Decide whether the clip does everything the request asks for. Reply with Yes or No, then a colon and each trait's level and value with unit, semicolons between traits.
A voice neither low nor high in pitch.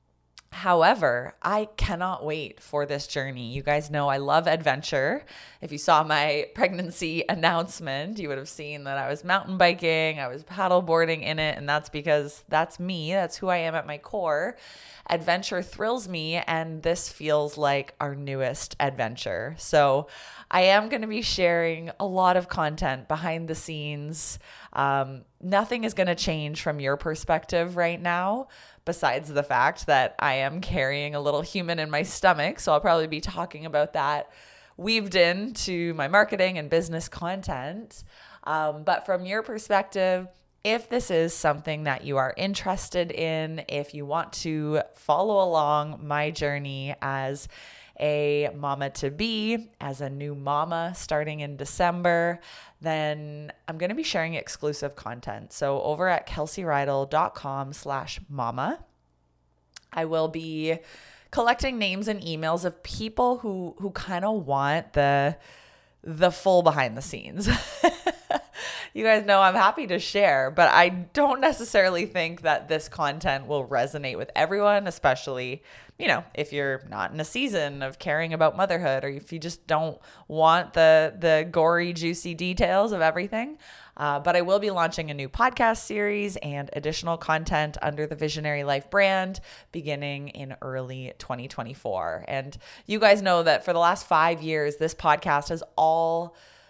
Yes: medium, 160 Hz